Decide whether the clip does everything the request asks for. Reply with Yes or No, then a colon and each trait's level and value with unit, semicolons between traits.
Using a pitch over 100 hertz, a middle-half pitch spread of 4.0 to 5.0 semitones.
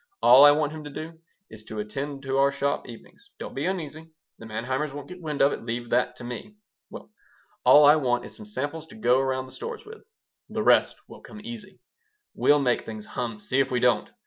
Yes: medium, 140 Hz; average, 4.3 semitones